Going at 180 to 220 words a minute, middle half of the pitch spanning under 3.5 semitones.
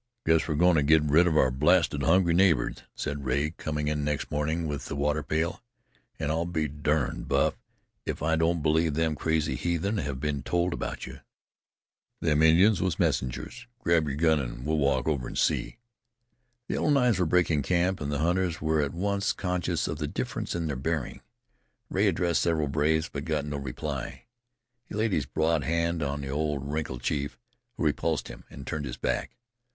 Yes: average, 190 wpm; average, 2.7 semitones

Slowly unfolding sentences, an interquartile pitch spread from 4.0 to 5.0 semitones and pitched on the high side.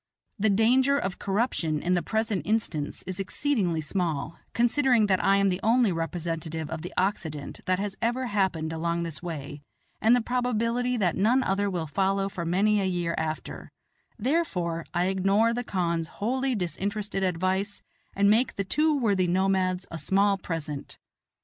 No: average, 160 wpm; average, 4.6 semitones; high, 195 Hz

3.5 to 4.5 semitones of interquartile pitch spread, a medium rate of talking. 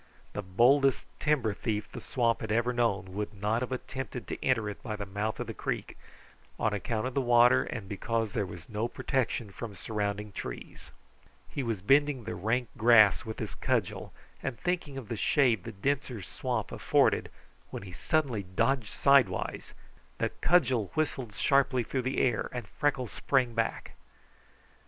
Yes: average, 3.9 semitones; average, 170 wpm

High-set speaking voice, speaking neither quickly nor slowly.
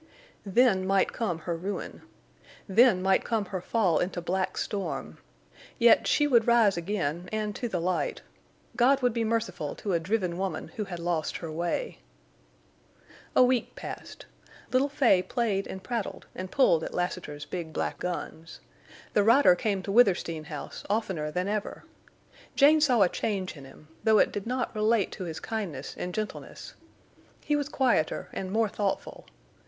Yes: high, 195 Hz; average, 165 wpm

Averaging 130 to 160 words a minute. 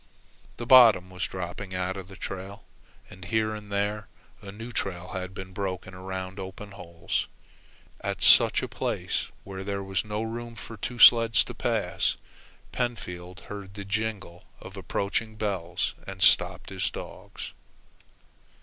Yes: average, 150 wpm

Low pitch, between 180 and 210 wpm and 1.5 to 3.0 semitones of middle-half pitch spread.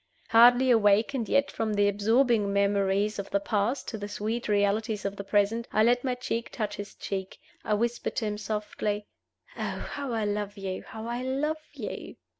No: high, 215 Hz; average, 185 wpm; average, 2.7 semitones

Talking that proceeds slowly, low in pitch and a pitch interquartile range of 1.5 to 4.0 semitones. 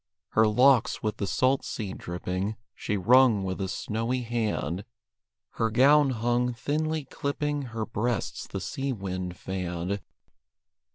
No: slow, 130 wpm; low, 115 Hz; average, 4.8 semitones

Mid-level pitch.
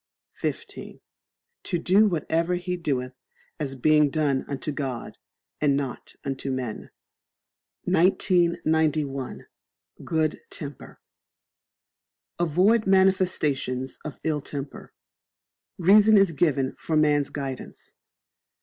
Yes: medium, 155 Hz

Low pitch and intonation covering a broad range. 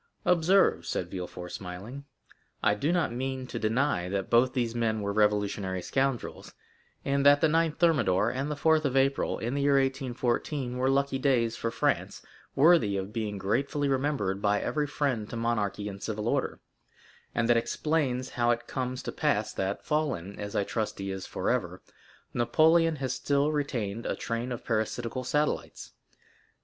No: low, 125 Hz; average, 5.0 semitones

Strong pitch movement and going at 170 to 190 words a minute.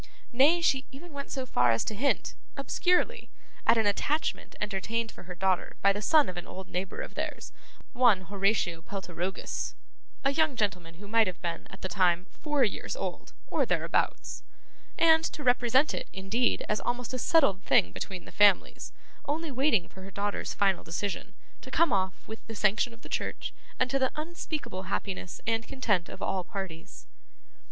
Yes: wide, 6.1 semitones; average, 180 wpm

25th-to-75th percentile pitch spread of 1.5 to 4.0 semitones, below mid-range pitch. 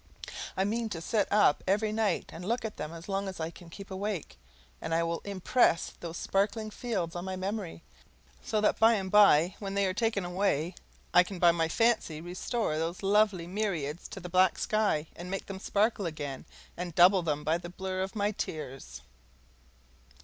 No: average, 3.6 semitones; high, 190 Hz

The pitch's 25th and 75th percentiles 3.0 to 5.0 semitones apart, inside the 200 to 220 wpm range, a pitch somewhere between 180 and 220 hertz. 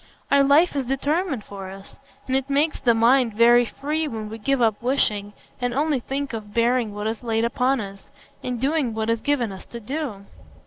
No: average, 3.9 semitones; fast, 205 wpm; high, 240 Hz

